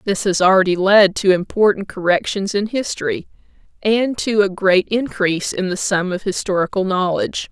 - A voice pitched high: Yes, high, 195 Hz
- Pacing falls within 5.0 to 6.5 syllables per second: Yes, 5.1 syllables/s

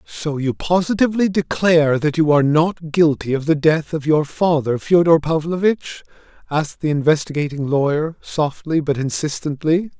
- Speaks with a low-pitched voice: No, medium, 155 Hz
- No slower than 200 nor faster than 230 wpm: No, average, 145 wpm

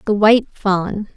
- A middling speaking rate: Yes, average, 155 wpm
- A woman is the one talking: Yes, female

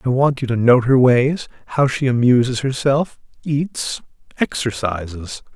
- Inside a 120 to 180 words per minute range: Yes, average, 140 wpm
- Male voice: Yes, male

